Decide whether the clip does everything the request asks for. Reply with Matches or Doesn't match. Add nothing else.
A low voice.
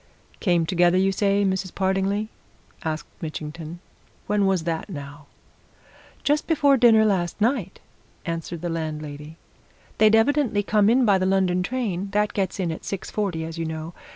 Doesn't match